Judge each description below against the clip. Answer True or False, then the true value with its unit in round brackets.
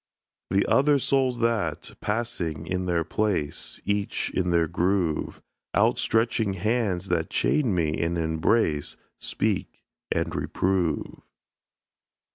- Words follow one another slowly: True (110 wpm)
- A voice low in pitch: True (95 Hz)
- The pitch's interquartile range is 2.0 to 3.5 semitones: False (5.1 semitones)